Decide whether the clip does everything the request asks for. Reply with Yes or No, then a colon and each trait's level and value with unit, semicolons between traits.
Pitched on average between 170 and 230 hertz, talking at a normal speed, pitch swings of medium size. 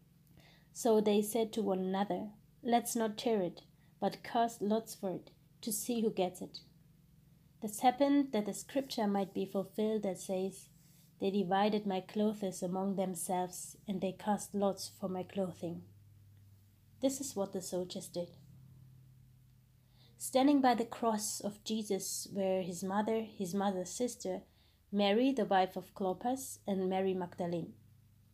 Yes: high, 190 Hz; average, 145 wpm; average, 4.9 semitones